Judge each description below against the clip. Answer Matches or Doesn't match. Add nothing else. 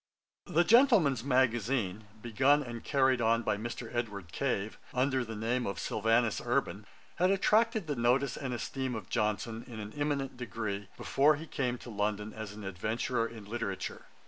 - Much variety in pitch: Doesn't match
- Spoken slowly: Doesn't match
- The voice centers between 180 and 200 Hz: Doesn't match